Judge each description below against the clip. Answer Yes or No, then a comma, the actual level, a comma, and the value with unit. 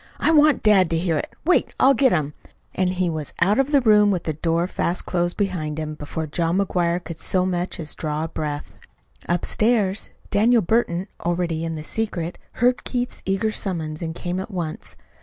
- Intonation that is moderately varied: Yes, average, 4.3 semitones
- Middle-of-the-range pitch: Yes, medium, 180 Hz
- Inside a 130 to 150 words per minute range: No, average, 195 wpm